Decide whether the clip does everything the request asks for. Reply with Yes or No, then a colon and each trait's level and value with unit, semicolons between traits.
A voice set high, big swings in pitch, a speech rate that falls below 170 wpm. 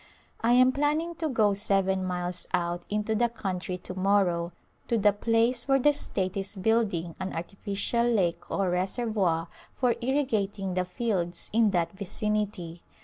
No: high, 200 Hz; average, 4.2 semitones; average, 155 wpm